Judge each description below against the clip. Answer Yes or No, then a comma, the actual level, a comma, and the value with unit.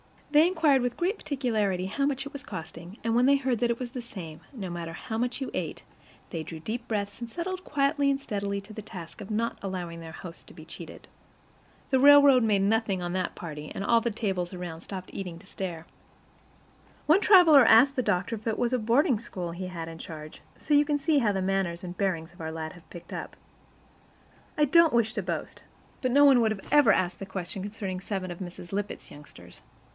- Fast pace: Yes, fast, 225 wpm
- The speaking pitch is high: Yes, high, 210 Hz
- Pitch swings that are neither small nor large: No, wide, 6.3 semitones